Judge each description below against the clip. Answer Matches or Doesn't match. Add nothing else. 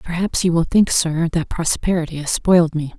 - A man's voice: Doesn't match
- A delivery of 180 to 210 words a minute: Matches